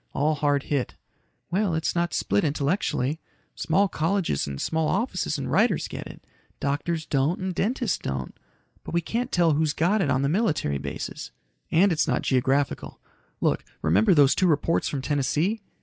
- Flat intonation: No, average, 4.3 semitones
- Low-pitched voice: No, medium, 155 Hz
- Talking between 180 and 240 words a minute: No, average, 165 wpm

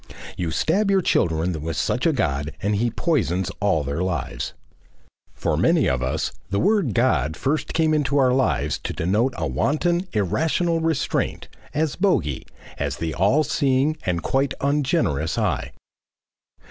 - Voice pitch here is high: No, low, 115 Hz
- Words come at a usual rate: Yes, average, 150 wpm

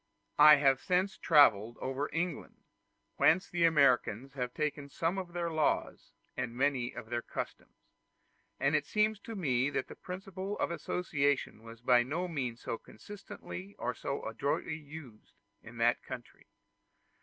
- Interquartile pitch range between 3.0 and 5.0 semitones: No, wide, 5.6 semitones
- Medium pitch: Yes, medium, 145 Hz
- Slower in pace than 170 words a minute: Yes, average, 150 wpm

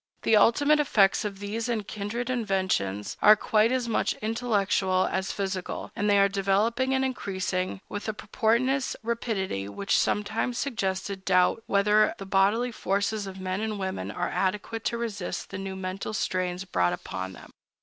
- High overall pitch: Yes, high, 200 Hz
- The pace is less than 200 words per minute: Yes, average, 165 wpm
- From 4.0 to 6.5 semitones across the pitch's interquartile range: No, average, 3.1 semitones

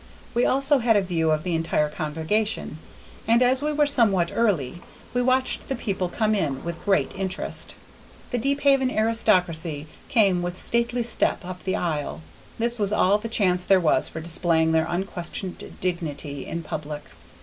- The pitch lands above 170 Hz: Yes, medium, 185 Hz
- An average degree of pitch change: No, wide, 6.1 semitones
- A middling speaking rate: Yes, average, 165 wpm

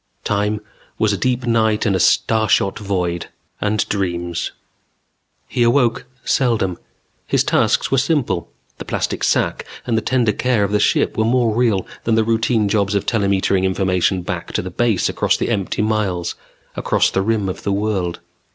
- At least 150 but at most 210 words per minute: Yes, average, 170 wpm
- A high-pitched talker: No, low, 105 Hz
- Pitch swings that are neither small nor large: Yes, average, 3.0 semitones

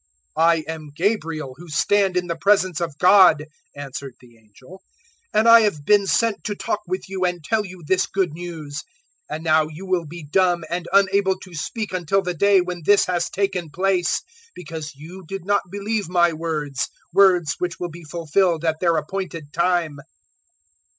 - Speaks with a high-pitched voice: No, medium, 175 Hz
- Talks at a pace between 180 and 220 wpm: Yes, average, 185 wpm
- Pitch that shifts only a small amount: No, average, 3.5 semitones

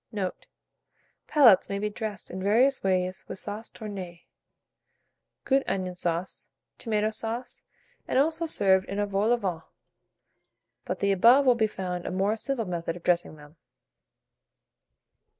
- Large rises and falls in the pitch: No, average, 3.8 semitones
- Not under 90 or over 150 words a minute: Yes, average, 145 wpm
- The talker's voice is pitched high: Yes, high, 200 Hz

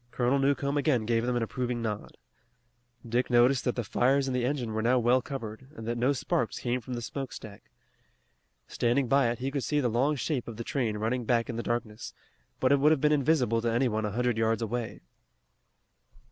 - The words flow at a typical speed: No, fast, 215 wpm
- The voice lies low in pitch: Yes, low, 120 Hz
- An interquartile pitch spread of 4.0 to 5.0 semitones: No, average, 2.7 semitones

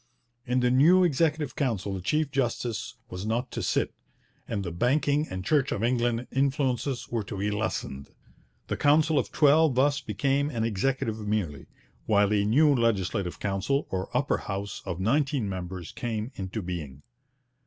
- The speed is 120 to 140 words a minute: No, average, 160 wpm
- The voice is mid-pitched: No, low, 115 Hz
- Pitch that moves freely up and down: Yes, wide, 6.0 semitones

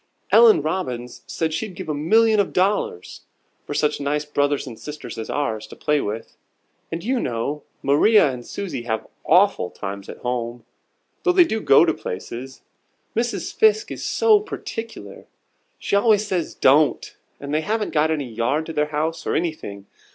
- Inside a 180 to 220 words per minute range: No, average, 170 wpm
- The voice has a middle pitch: Yes, medium, 150 Hz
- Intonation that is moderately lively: No, wide, 8.3 semitones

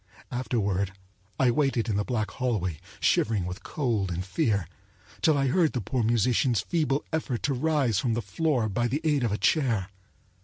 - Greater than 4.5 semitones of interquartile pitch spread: Yes, average, 5.0 semitones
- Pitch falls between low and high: No, low, 120 Hz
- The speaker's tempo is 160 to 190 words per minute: Yes, average, 180 wpm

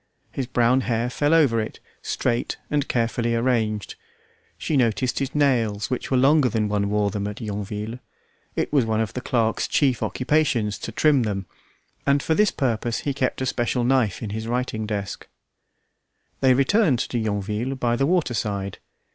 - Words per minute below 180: Yes, average, 170 wpm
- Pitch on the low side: Yes, low, 120 Hz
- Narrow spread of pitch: No, average, 3.7 semitones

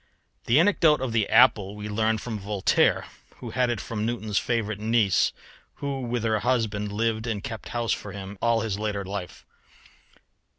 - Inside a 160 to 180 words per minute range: Yes, average, 170 wpm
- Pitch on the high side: No, low, 110 Hz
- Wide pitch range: No, narrow, 2.4 semitones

